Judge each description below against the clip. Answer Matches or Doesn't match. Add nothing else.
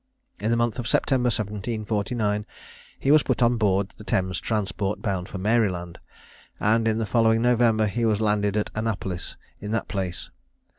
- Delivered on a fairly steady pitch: Matches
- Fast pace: Doesn't match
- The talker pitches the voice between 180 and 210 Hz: Doesn't match